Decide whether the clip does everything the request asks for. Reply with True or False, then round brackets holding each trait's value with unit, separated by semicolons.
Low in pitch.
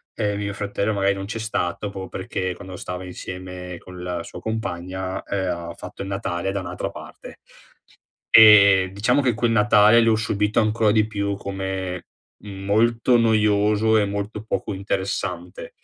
True (100 Hz)